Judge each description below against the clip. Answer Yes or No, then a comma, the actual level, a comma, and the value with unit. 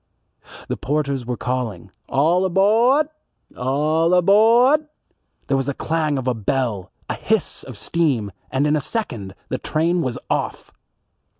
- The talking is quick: No, average, 140 wpm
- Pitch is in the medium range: Yes, medium, 150 Hz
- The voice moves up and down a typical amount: No, wide, 6.0 semitones